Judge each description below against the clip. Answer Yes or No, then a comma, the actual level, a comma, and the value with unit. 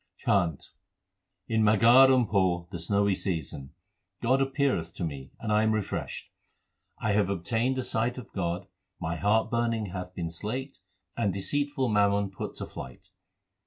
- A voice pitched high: No, low, 105 Hz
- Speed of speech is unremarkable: Yes, average, 155 wpm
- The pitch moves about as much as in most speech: Yes, average, 4.8 semitones